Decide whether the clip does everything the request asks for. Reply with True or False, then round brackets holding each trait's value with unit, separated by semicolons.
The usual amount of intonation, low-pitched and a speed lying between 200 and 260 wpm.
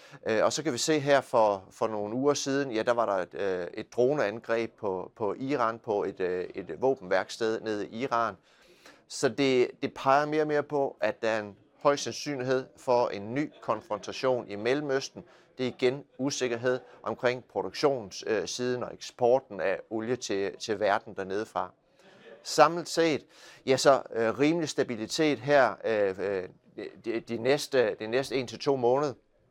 False (4.0 semitones; 130 Hz; 165 wpm)